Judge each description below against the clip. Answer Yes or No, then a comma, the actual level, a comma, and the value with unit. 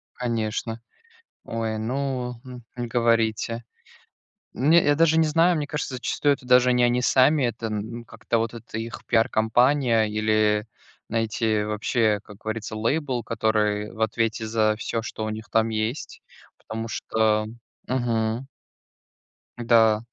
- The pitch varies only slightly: Yes, narrow, 2.3 semitones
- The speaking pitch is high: No, low, 115 Hz